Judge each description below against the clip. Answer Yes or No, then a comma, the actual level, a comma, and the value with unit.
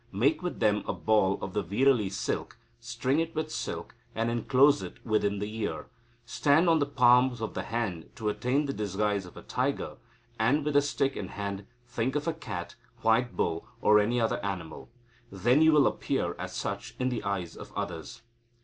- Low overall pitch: Yes, low, 115 Hz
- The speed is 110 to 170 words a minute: No, average, 195 wpm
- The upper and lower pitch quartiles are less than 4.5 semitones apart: No, average, 5.0 semitones